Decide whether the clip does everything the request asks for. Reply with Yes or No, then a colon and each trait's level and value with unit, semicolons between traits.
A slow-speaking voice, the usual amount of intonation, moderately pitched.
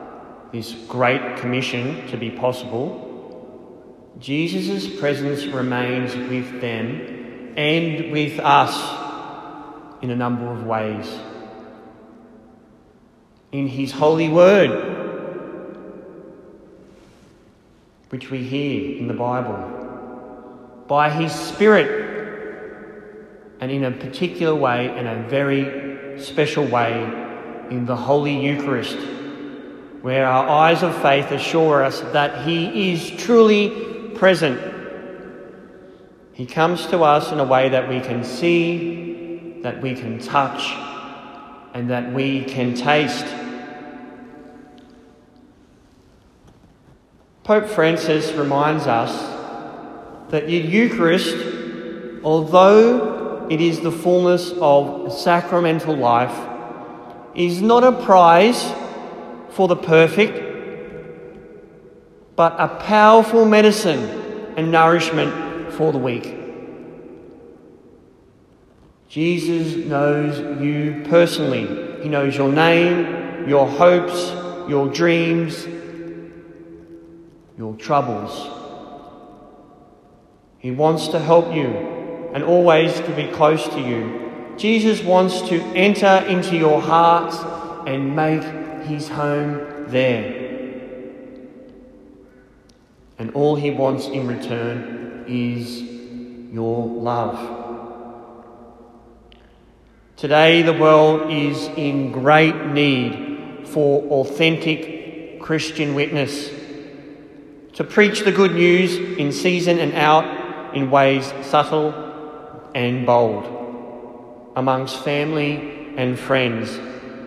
Yes: slow, 95 wpm; average, 5.0 semitones; medium, 145 Hz